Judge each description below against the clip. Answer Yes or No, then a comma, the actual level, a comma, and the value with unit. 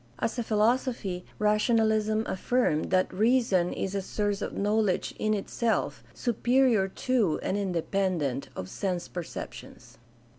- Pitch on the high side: Yes, high, 210 Hz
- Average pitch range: Yes, average, 3.5 semitones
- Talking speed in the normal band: No, slow, 120 wpm